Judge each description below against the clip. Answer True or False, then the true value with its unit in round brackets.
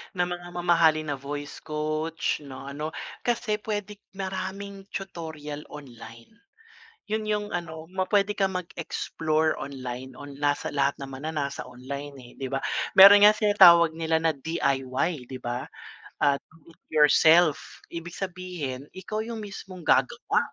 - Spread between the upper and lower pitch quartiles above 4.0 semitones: True (5.0 semitones)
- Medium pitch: True (160 Hz)